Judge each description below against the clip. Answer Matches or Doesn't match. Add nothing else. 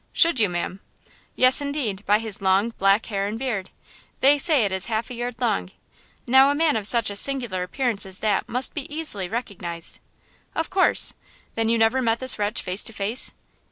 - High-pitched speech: Matches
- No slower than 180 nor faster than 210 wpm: Matches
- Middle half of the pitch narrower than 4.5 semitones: Doesn't match